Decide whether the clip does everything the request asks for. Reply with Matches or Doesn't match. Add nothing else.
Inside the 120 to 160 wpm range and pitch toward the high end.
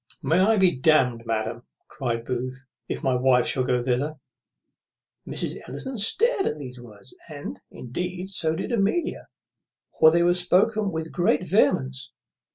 Doesn't match